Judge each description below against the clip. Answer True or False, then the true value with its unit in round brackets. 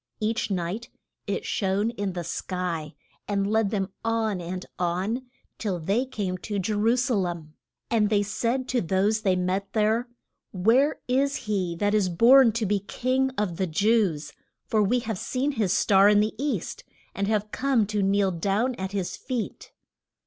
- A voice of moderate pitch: False (205 Hz)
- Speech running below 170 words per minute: False (175 wpm)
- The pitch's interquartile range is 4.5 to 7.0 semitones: False (3.4 semitones)